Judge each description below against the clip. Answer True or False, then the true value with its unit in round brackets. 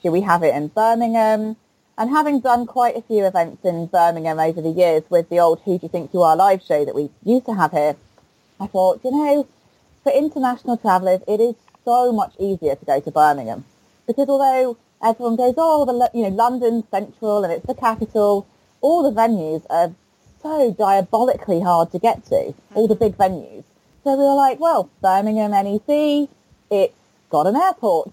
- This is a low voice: False (220 Hz)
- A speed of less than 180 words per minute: False (190 wpm)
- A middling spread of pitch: False (5.9 semitones)